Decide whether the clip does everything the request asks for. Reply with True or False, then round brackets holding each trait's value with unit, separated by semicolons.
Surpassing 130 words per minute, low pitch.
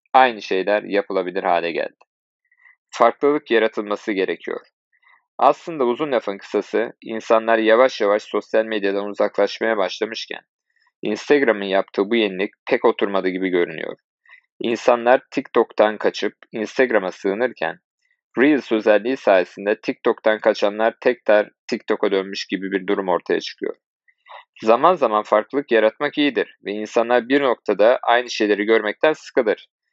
False (115 wpm; 110 Hz)